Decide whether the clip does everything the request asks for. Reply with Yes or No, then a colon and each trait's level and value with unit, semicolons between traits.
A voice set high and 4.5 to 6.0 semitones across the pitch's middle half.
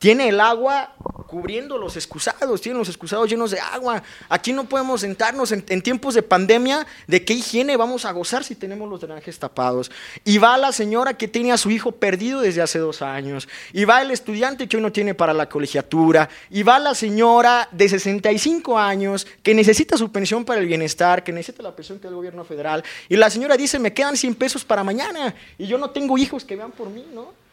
Yes: high, 220 Hz; average, 5.2 semitones